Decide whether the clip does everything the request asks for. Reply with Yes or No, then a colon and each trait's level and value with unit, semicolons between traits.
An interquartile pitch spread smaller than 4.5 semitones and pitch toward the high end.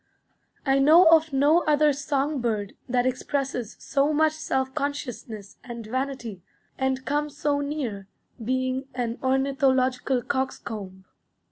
Yes: average, 2.8 semitones; very high, 265 Hz